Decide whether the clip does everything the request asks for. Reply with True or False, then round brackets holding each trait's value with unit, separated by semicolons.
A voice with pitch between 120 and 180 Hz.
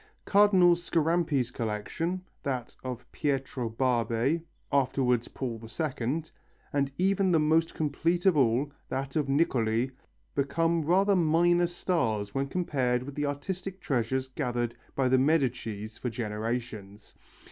True (135 Hz)